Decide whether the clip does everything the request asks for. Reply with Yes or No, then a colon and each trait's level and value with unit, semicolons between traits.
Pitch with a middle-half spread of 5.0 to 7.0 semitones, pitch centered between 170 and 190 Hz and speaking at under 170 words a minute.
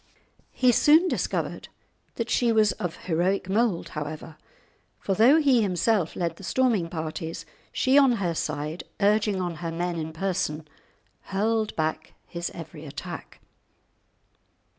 Yes: wide, 5.5 semitones; medium, 185 Hz; slow, 135 wpm